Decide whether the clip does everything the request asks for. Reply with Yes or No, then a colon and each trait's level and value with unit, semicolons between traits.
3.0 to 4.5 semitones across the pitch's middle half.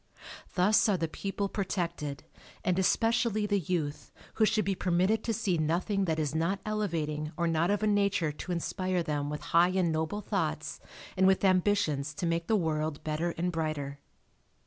Yes: average, 4.1 semitones